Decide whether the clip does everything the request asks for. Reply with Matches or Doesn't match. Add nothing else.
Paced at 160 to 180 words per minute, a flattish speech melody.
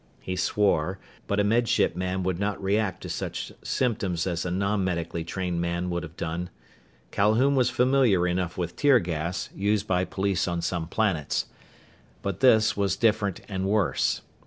Doesn't match